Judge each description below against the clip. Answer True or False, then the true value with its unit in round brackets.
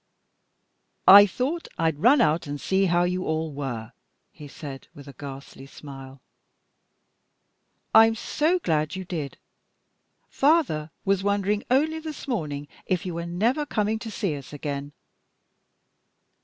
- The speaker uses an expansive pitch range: True (7.3 semitones)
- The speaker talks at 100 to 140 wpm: True (135 wpm)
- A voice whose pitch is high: False (175 Hz)